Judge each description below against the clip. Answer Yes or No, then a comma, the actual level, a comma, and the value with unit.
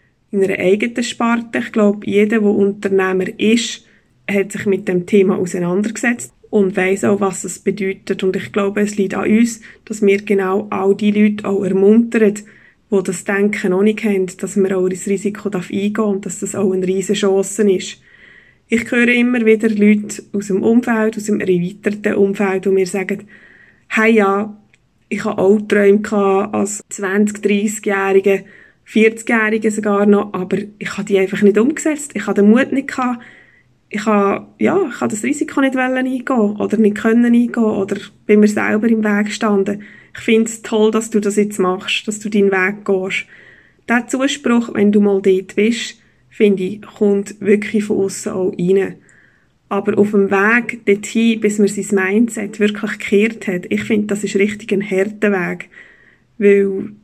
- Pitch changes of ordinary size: No, narrow, 1.9 semitones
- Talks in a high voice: Yes, high, 205 Hz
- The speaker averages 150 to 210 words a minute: Yes, average, 180 wpm